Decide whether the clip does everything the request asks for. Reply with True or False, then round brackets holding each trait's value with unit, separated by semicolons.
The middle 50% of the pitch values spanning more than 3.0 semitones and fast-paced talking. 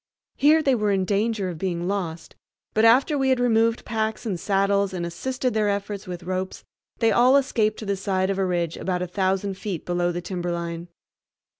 False (3.8 semitones; 195 wpm)